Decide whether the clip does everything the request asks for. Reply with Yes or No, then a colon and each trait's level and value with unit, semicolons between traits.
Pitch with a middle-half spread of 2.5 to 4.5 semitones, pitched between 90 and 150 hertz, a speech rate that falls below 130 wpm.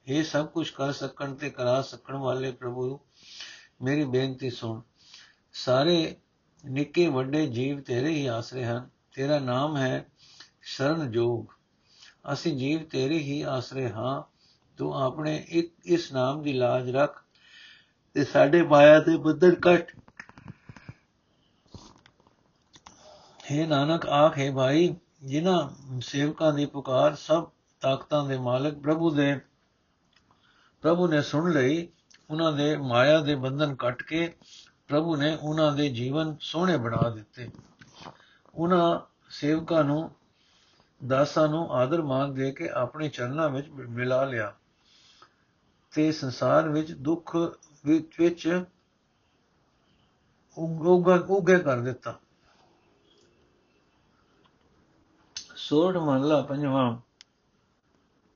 Yes: average, 3.4 semitones; medium, 145 Hz; average, 110 wpm